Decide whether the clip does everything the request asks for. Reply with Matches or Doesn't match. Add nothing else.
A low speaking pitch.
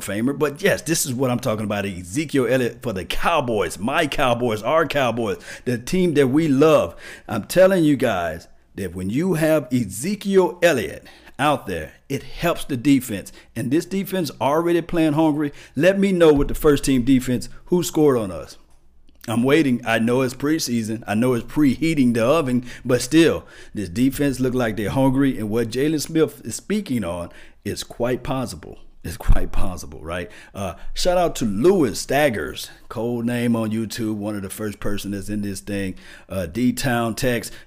Matches